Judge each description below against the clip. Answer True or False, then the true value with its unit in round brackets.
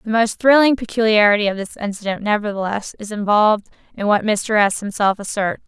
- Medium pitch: False (210 Hz)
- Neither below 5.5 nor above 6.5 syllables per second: True (5.7 syllables/s)